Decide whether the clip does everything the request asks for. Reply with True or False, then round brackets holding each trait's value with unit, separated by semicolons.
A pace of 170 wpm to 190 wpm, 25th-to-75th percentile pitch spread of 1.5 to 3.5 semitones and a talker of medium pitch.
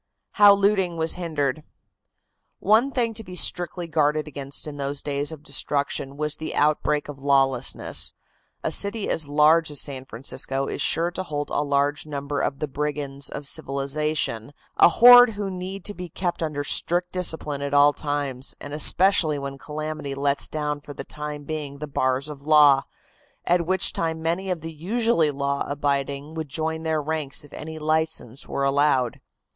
True (175 wpm; 2.6 semitones; 150 Hz)